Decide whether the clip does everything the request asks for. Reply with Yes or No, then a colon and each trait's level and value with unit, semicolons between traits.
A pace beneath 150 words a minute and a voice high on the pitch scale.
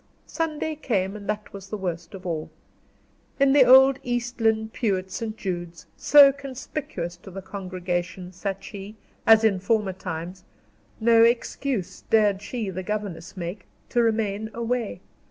No: average, 155 wpm; high, 205 Hz